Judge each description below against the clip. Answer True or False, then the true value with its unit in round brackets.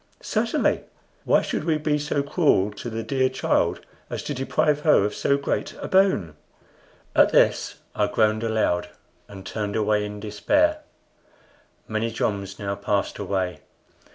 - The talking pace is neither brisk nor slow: True (150 wpm)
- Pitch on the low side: True (110 Hz)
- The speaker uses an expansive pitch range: True (5.9 semitones)